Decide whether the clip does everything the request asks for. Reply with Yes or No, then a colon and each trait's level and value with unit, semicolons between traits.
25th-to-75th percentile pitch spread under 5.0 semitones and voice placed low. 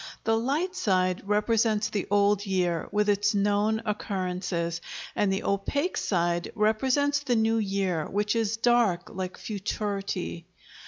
No: average, 3.0 semitones; high, 205 Hz